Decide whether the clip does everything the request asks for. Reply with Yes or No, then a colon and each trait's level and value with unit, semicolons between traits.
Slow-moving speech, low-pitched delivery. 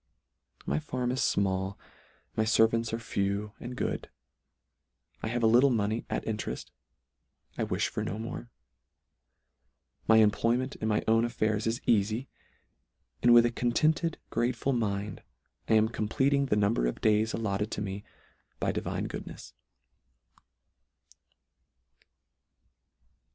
Yes: slow, 130 wpm; low, 110 Hz